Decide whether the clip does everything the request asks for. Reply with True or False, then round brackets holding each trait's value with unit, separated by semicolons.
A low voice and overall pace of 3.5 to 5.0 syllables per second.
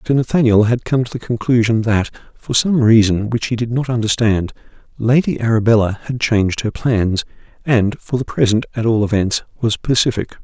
False (115 Hz; 5.4 syllables/s)